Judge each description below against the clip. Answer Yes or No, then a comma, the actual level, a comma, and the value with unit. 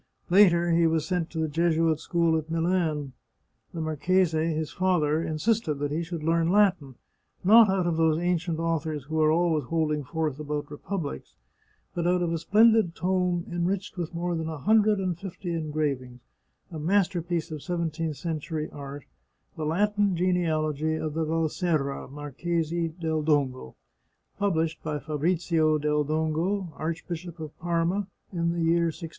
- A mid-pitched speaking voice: Yes, medium, 165 Hz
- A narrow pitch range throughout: Yes, narrow, 2.2 semitones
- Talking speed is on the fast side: No, average, 155 wpm